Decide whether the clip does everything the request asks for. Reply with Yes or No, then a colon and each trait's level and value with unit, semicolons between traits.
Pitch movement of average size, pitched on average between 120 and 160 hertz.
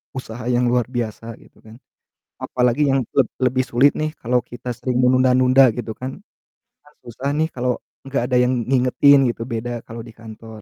No: narrow, 1.8 semitones; low, 125 Hz